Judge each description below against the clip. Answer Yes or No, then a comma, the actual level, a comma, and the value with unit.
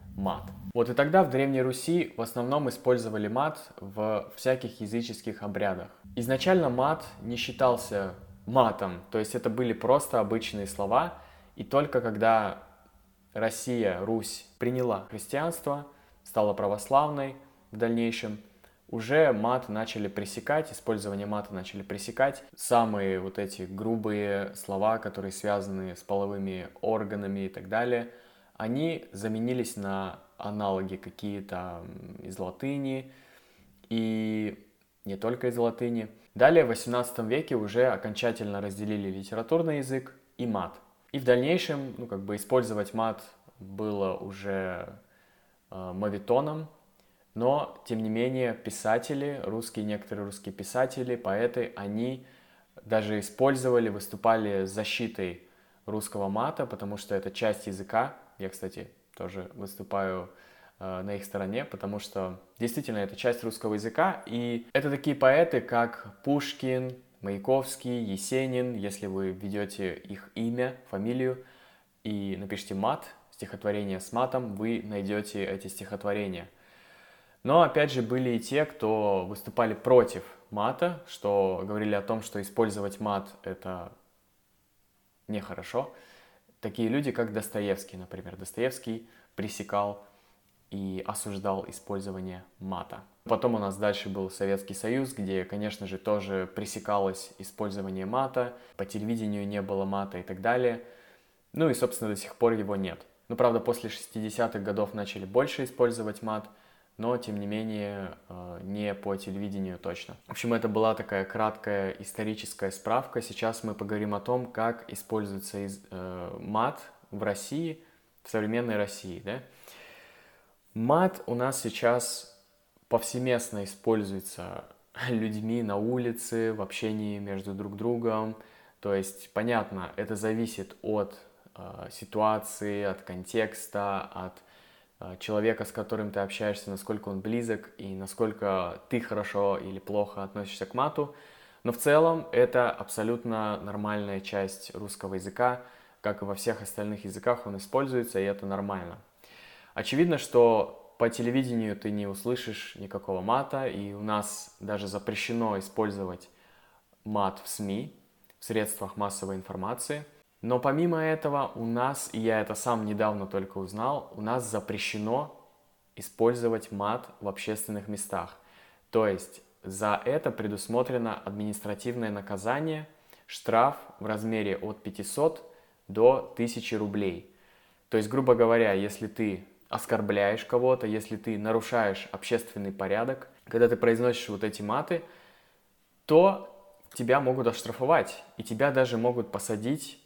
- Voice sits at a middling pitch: No, low, 105 Hz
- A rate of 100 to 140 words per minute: Yes, average, 125 wpm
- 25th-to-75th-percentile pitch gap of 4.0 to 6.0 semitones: No, average, 3.4 semitones